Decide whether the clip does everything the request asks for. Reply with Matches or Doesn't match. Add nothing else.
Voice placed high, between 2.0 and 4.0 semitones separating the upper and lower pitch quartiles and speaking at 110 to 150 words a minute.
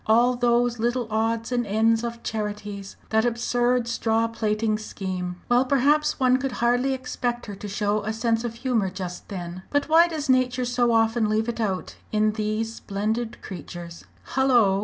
Doesn't match